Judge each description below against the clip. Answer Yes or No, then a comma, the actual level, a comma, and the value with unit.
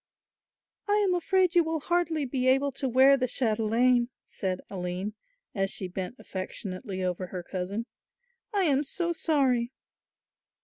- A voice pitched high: Yes, very high, 250 Hz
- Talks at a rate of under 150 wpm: Yes, average, 140 wpm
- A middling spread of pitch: No, wide, 8.0 semitones